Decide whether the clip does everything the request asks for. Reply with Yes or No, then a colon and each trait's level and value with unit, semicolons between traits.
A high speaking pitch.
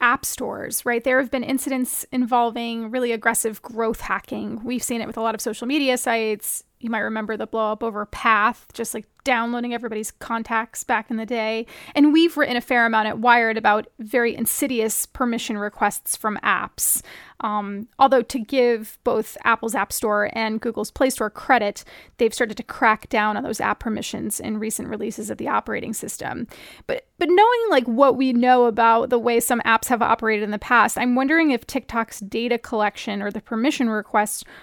Yes: high, 230 Hz